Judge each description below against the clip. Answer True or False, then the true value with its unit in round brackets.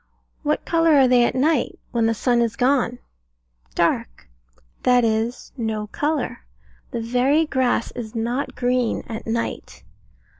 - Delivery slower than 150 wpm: True (140 wpm)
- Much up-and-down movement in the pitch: False (2.8 semitones)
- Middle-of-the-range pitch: False (245 Hz)